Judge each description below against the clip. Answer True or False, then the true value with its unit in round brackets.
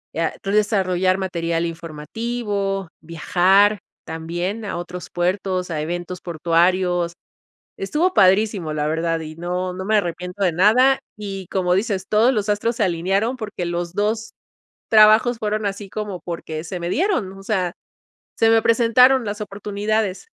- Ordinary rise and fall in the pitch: True (3.5 semitones)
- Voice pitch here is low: False (190 Hz)